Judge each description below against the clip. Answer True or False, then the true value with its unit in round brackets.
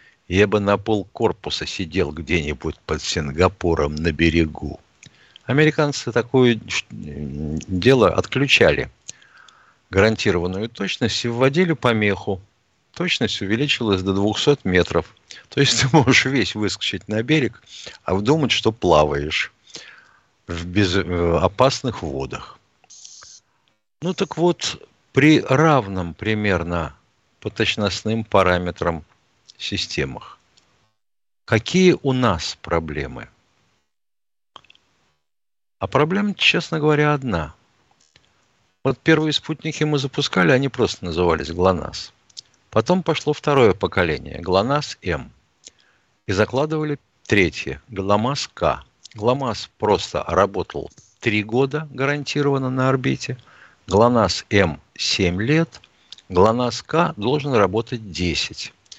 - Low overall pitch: True (110 Hz)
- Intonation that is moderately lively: False (7.0 semitones)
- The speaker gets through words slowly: True (95 wpm)